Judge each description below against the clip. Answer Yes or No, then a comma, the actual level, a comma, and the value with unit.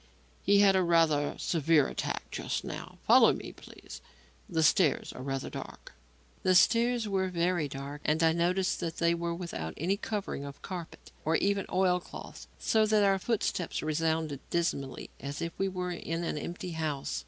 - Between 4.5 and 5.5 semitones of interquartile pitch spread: No, average, 3.5 semitones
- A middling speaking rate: Yes, average, 175 wpm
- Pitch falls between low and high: Yes, medium, 170 Hz